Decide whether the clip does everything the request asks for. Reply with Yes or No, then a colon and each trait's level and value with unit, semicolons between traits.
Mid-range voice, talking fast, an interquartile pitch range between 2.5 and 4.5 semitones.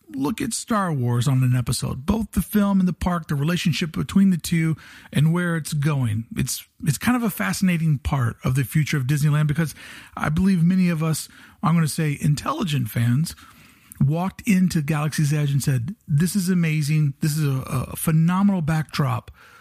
No: medium, 160 Hz; average, 185 wpm; average, 4.1 semitones